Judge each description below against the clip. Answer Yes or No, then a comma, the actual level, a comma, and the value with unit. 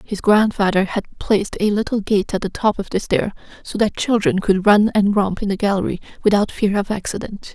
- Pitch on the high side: Yes, high, 205 Hz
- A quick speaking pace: Yes, fast, 215 wpm